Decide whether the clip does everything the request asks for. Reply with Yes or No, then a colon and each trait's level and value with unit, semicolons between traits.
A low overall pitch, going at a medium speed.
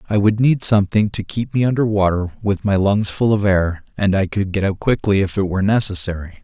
No: low, 100 Hz; fast, 235 wpm